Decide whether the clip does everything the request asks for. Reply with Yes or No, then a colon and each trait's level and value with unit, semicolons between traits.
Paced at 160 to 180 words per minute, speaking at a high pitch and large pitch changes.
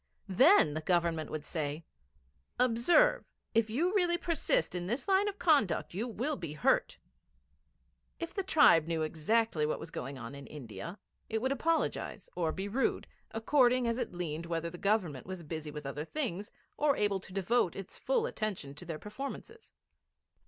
Yes: average, 170 wpm; high, 195 Hz; wide, 8.7 semitones